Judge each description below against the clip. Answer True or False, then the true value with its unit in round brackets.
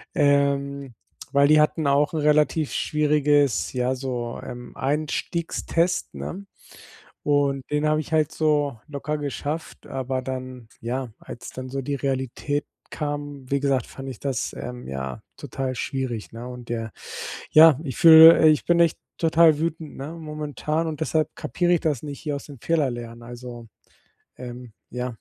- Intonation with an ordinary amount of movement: True (3.1 semitones)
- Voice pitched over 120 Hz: True (140 Hz)